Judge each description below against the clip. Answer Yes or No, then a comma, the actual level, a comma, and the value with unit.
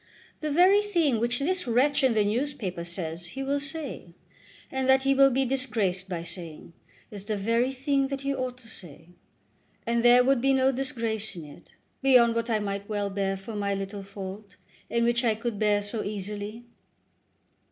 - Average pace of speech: Yes, average, 185 wpm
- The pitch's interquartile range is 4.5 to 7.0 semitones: Yes, average, 5.1 semitones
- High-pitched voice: Yes, high, 230 Hz